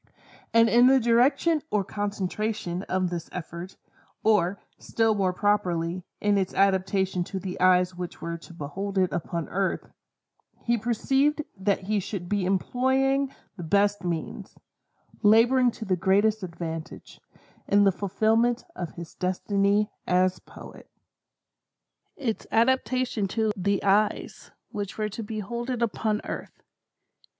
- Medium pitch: No, high, 200 Hz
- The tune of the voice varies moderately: Yes, average, 3.6 semitones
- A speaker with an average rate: No, slow, 130 wpm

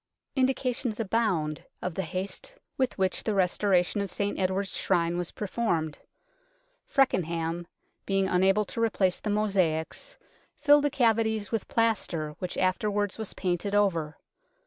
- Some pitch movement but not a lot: Yes, average, 3.9 semitones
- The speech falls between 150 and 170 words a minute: No, slow, 135 wpm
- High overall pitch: Yes, high, 195 Hz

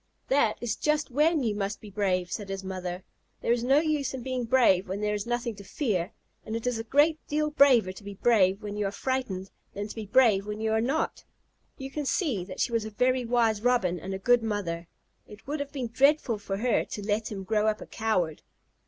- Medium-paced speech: No, fast, 235 wpm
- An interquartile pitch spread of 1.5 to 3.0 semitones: No, average, 4.4 semitones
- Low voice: No, high, 220 Hz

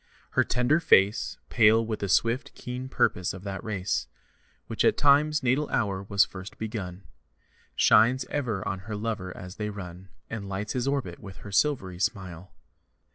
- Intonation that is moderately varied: Yes, average, 4.5 semitones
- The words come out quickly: No, average, 165 wpm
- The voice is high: No, low, 105 Hz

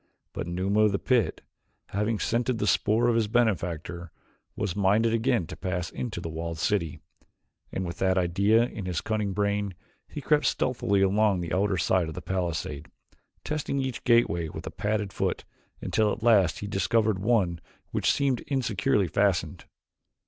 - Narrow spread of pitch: No, average, 4.1 semitones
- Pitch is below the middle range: Yes, low, 100 Hz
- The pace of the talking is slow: No, average, 165 wpm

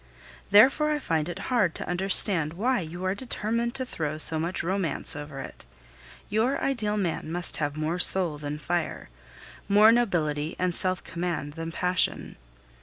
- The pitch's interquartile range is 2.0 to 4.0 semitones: No, average, 4.9 semitones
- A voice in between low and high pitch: Yes, medium, 180 Hz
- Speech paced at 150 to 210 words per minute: Yes, average, 160 wpm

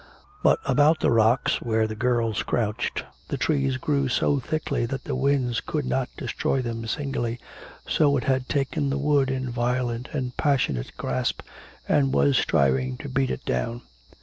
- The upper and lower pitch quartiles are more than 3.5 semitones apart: No, average, 3.2 semitones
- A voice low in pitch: Yes, low, 130 Hz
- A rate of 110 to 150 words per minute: No, average, 165 wpm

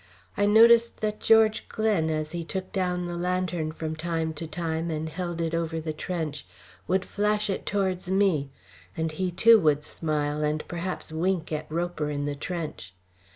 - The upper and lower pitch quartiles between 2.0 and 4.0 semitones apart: Yes, average, 3.2 semitones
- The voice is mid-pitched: Yes, medium, 170 Hz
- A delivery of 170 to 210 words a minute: Yes, average, 175 wpm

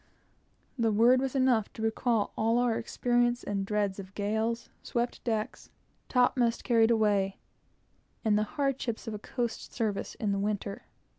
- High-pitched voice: Yes, high, 225 Hz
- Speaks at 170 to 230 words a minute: No, average, 150 wpm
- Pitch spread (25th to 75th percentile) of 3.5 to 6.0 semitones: No, narrow, 2.5 semitones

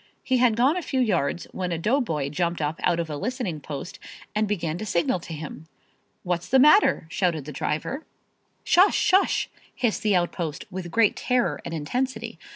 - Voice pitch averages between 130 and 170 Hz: No, medium, 180 Hz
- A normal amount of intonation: No, wide, 7.4 semitones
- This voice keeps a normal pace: Yes, average, 180 wpm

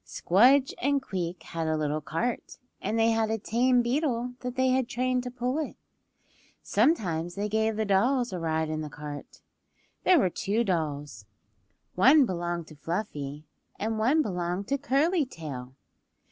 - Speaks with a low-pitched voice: No, high, 215 Hz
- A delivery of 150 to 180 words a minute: Yes, average, 160 wpm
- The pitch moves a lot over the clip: Yes, wide, 7.4 semitones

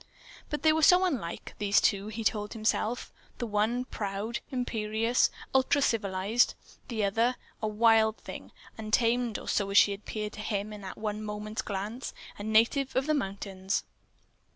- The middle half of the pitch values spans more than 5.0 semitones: No, average, 2.8 semitones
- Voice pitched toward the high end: Yes, high, 215 Hz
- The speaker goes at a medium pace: Yes, average, 160 wpm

